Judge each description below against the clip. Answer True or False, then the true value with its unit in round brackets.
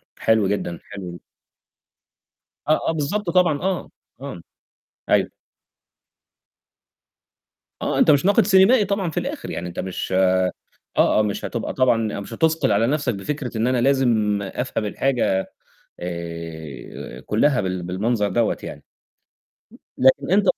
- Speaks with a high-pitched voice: False (115 Hz)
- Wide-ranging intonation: True (7.8 semitones)